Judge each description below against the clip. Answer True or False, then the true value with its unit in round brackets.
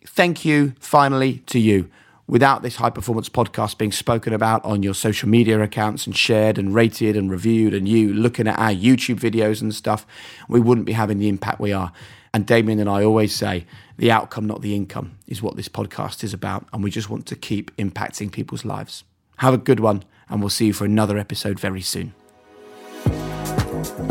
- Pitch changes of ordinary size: False (2.2 semitones)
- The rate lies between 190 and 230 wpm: True (200 wpm)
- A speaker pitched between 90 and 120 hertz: True (110 Hz)